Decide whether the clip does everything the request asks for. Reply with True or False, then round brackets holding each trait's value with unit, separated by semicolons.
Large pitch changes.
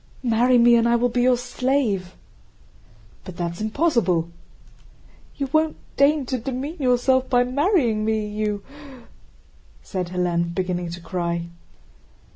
True (5.9 semitones)